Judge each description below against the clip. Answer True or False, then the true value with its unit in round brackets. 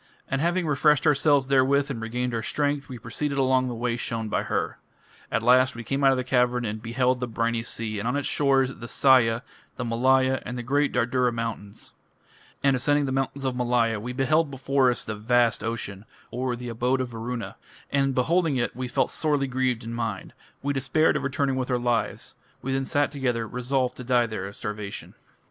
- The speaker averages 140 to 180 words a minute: False (205 wpm)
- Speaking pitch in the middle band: False (125 Hz)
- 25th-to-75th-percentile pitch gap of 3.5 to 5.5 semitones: False (2.7 semitones)